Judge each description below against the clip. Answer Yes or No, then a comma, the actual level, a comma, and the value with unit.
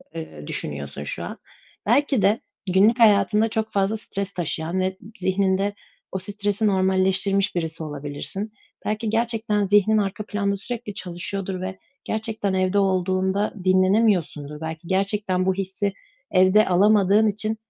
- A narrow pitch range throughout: Yes, narrow, 2.2 semitones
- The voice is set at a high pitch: Yes, high, 195 Hz